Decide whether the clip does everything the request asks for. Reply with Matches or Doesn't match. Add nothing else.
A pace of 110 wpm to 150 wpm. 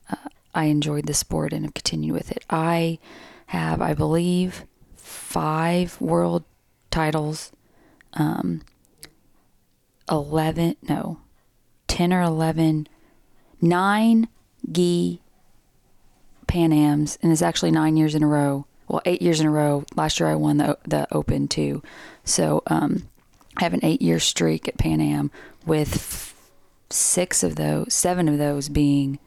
Matches